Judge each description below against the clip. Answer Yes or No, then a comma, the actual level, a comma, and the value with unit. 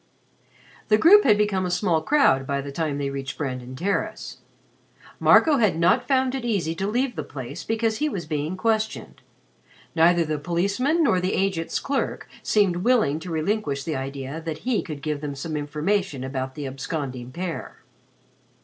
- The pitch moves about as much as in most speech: No, wide, 6.8 semitones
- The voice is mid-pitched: Yes, medium, 170 Hz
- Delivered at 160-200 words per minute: Yes, average, 170 wpm